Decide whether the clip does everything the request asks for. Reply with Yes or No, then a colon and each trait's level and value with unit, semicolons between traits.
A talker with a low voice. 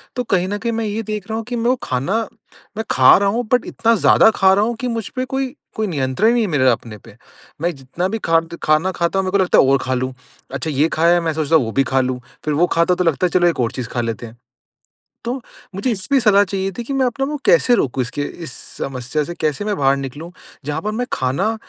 No: medium, 175 Hz